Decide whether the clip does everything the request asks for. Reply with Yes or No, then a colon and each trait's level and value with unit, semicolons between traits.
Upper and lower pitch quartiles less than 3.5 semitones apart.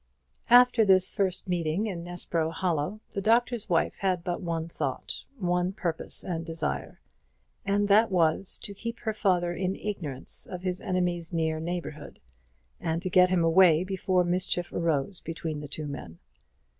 Yes: average, 2.7 semitones